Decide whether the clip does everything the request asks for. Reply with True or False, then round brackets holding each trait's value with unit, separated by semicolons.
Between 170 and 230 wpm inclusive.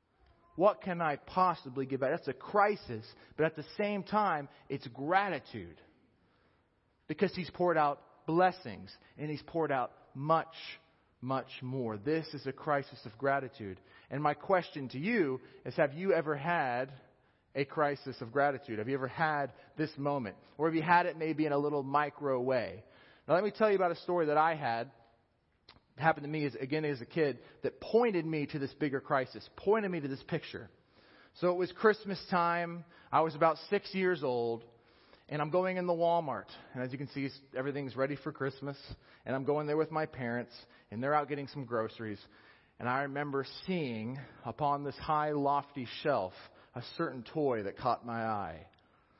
True (185 wpm)